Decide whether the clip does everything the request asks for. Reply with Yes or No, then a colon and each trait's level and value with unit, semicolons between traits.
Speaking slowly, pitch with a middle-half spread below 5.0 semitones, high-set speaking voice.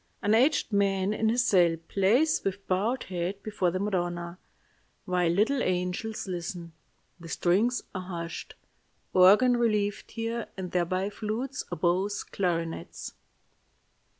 Yes: slow, 125 wpm; average, 3.6 semitones; high, 195 Hz